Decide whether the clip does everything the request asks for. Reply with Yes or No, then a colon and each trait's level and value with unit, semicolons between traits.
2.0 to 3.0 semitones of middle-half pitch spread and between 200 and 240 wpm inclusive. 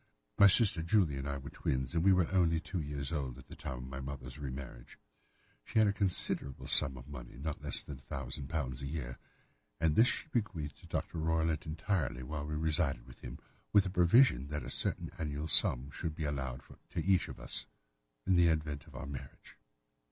No: average, 3.8 semitones; fast, 205 wpm